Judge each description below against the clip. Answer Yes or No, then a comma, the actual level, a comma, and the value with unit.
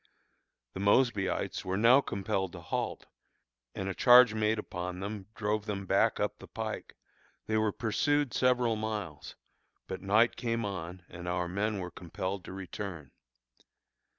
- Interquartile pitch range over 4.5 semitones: No, average, 3.1 semitones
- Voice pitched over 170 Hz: No, low, 100 Hz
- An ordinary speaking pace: Yes, average, 150 wpm